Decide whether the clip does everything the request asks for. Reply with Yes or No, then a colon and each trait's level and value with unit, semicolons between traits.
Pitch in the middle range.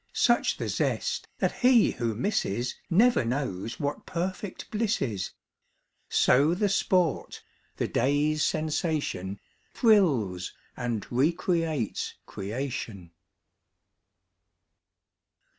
Yes: medium, 145 Hz